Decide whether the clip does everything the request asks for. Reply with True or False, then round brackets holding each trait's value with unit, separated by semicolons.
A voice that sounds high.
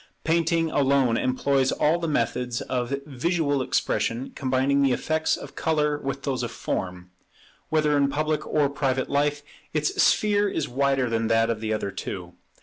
False (140 Hz)